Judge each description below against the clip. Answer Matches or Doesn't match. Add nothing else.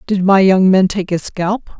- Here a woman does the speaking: Matches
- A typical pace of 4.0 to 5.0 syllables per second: Matches